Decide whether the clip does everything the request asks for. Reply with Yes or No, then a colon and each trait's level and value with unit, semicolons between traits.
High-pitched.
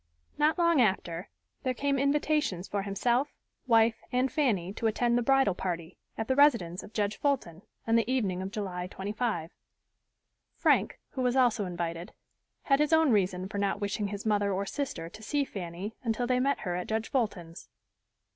Yes: high, 215 Hz